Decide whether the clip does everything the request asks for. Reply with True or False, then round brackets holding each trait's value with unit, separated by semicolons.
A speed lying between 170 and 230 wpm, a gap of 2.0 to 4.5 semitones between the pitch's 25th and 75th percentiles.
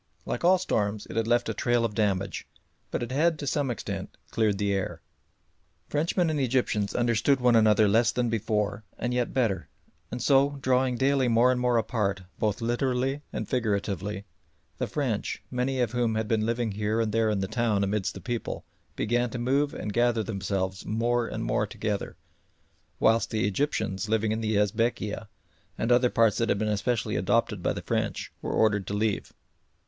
True (185 wpm; 2.9 semitones)